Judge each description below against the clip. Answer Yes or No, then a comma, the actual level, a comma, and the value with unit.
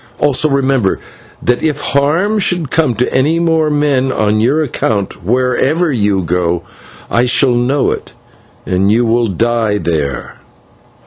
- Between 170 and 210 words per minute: No, average, 145 wpm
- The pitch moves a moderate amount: No, wide, 5.7 semitones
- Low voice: Yes, low, 125 Hz